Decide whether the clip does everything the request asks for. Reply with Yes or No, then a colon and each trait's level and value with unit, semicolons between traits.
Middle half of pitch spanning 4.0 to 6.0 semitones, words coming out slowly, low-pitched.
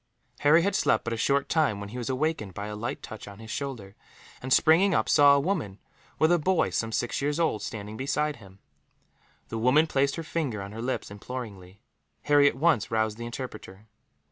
No: wide, 5.5 semitones; fast, 205 wpm; low, 125 Hz